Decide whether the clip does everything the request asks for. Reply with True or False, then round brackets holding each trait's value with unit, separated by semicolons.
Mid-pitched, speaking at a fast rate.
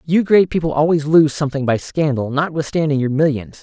False (150 Hz; 180 wpm)